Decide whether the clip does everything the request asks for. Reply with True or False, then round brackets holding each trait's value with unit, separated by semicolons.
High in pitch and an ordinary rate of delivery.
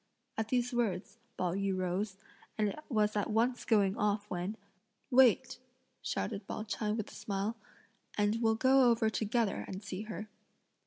True (215 Hz; 155 wpm)